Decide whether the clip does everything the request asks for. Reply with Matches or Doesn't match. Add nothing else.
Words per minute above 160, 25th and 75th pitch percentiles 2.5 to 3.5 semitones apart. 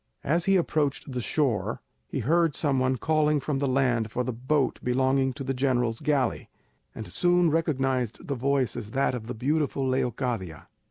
Matches